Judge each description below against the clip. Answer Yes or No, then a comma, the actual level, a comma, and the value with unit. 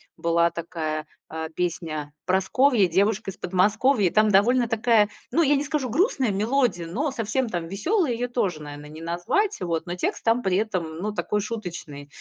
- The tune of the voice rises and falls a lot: Yes, wide, 6.3 semitones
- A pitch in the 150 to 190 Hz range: No, high, 200 Hz